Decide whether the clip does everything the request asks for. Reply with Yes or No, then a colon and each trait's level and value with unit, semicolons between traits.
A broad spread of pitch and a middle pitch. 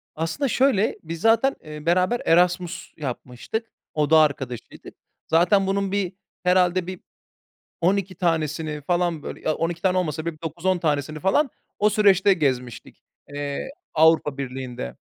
No: average, 3.8 semitones; medium, 170 Hz